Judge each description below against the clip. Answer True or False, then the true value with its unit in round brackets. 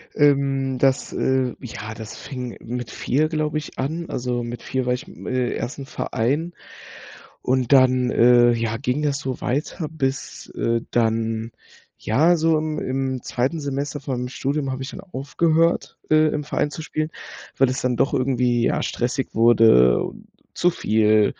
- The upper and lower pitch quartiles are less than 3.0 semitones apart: False (3.4 semitones)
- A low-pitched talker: True (130 Hz)